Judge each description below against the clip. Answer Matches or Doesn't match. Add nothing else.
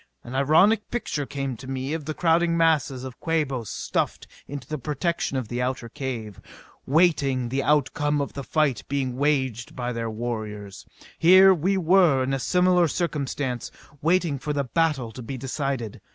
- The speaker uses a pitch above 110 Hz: Matches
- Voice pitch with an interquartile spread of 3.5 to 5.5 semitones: Matches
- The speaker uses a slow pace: Doesn't match